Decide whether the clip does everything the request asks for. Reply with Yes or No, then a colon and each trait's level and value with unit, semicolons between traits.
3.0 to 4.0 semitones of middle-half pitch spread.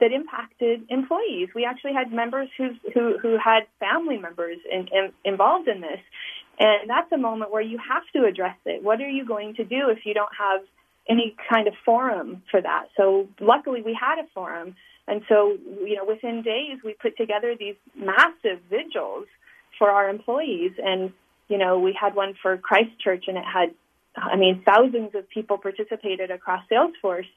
No: average, 4.8 semitones